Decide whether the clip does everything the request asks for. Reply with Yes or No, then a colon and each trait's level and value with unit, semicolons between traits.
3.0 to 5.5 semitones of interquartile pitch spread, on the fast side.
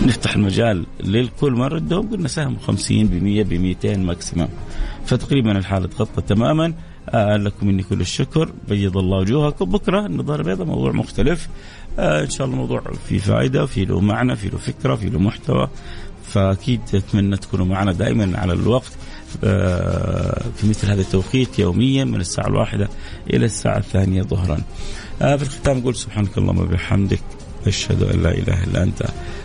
No: average, 4.4 semitones; average, 160 wpm